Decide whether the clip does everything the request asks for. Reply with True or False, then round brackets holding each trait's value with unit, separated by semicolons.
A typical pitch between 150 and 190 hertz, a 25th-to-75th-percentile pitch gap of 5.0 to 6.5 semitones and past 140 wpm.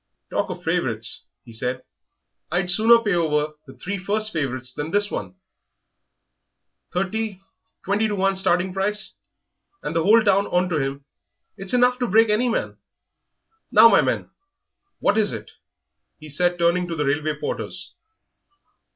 True (185 Hz; 5.3 semitones; 150 wpm)